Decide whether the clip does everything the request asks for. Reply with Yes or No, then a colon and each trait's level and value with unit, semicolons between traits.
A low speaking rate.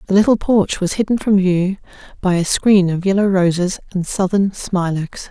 No: average, 180 wpm